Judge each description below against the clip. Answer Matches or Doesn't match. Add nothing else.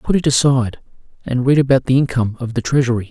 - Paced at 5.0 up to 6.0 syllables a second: Doesn't match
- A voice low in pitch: Matches